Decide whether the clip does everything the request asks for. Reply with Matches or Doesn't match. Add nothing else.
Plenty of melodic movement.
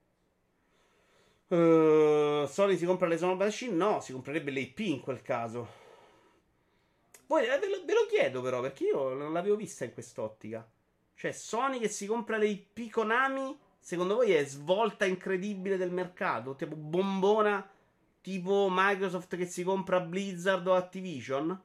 Doesn't match